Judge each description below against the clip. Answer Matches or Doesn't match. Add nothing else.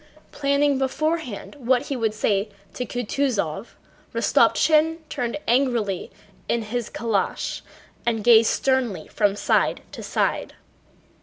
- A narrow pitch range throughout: Doesn't match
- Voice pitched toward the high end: Matches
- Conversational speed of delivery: Doesn't match